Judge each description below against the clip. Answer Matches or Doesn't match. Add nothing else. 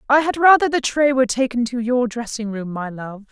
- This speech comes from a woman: Matches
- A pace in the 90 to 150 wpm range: Doesn't match